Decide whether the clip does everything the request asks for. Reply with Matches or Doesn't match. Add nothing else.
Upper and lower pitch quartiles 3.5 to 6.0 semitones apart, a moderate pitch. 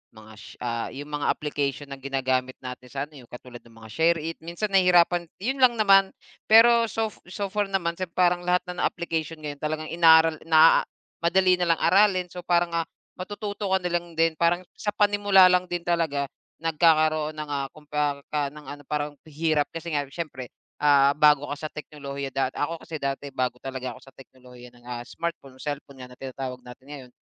Matches